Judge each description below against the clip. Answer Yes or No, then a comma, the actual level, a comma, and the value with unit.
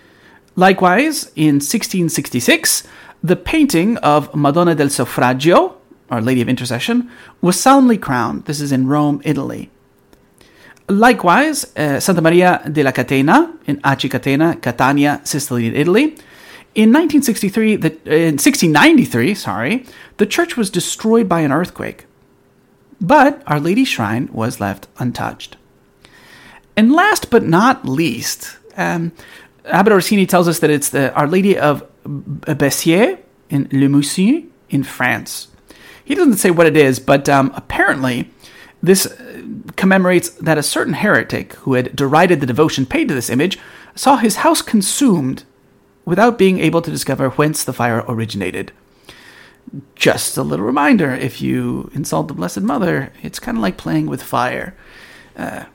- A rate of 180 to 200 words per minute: No, average, 140 wpm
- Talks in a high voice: No, medium, 165 Hz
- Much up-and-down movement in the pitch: Yes, wide, 7.6 semitones